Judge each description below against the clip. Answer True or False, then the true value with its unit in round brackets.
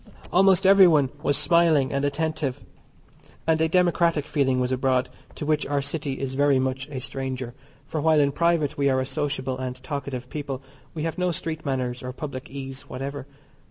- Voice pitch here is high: False (140 Hz)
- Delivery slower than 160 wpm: False (180 wpm)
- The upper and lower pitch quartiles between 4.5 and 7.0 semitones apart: False (3.1 semitones)